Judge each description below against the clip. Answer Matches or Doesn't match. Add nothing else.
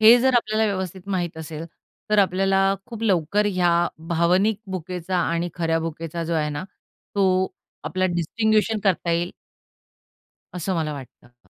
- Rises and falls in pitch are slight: Doesn't match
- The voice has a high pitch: Doesn't match